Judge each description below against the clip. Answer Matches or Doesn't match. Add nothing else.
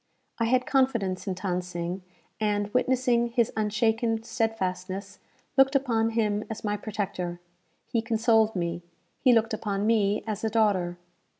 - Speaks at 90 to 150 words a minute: Matches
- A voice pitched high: Matches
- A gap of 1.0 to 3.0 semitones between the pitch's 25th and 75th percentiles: Matches